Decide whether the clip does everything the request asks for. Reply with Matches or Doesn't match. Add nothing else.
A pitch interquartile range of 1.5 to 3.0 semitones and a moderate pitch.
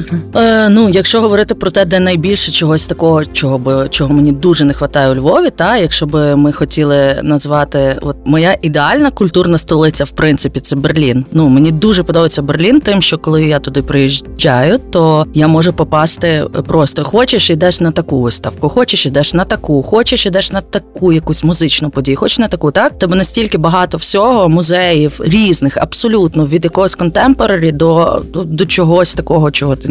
Doesn't match